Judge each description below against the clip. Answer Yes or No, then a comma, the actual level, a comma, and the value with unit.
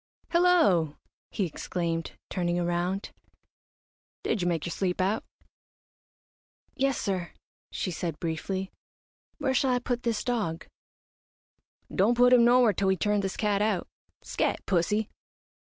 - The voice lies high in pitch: Yes, high, 195 Hz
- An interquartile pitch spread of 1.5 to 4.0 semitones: No, average, 5.2 semitones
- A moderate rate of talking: No, slow, 130 wpm